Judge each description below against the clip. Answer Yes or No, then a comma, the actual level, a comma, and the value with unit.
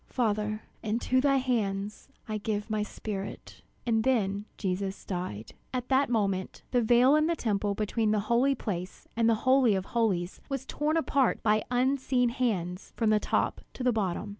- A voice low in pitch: No, high, 220 Hz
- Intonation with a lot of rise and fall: No, average, 3.8 semitones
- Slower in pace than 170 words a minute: No, average, 175 wpm